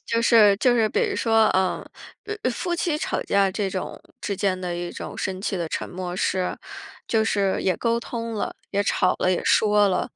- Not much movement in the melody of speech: No, average, 3.7 semitones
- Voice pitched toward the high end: Yes, high, 205 Hz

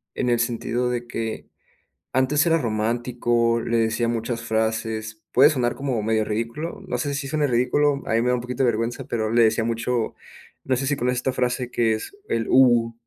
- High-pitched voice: No, low, 120 Hz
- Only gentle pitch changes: Yes, narrow, 1.9 semitones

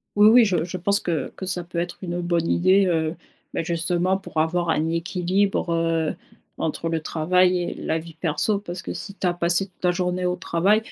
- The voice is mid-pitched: Yes, medium, 175 Hz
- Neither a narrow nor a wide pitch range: No, narrow, 1.9 semitones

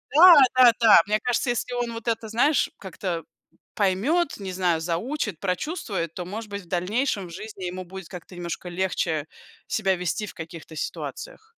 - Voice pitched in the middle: No, high, 195 Hz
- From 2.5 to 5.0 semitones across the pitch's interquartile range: Yes, average, 4.7 semitones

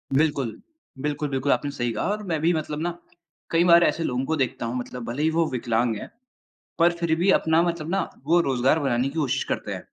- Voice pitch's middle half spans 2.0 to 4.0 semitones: No, average, 4.8 semitones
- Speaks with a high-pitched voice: No, medium, 150 Hz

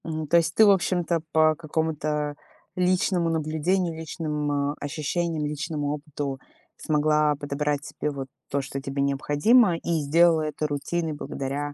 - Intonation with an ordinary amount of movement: No, narrow, 2.2 semitones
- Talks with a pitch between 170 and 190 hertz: No, medium, 155 Hz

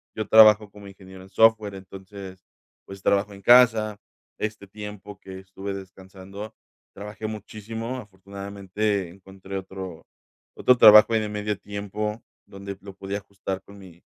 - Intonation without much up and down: Yes, narrow, 1.8 semitones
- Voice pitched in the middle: No, low, 100 Hz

